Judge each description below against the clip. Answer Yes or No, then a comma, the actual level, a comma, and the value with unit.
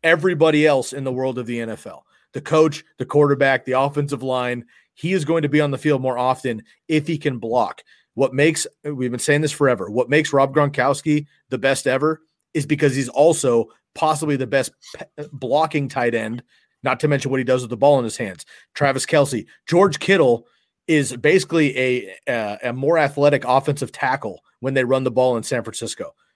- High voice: No, medium, 140 Hz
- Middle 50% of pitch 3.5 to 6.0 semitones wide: No, average, 2.8 semitones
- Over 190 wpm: Yes, average, 200 wpm